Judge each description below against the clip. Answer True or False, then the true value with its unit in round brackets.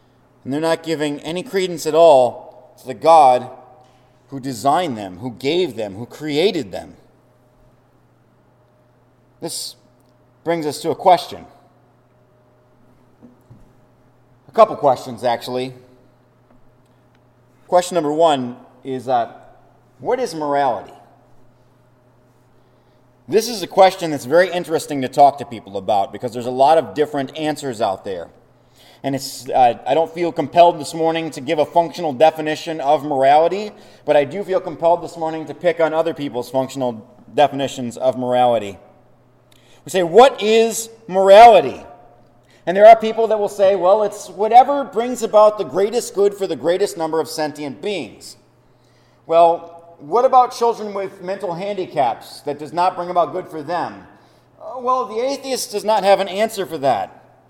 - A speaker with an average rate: True (150 wpm)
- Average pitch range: False (6.2 semitones)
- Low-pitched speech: False (150 Hz)